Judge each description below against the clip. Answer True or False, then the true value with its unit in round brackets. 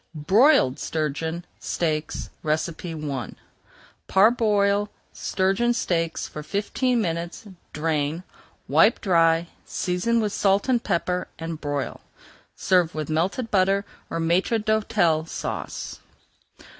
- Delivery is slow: True (100 wpm)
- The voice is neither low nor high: True (175 Hz)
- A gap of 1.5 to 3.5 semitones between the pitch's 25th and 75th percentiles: False (4.4 semitones)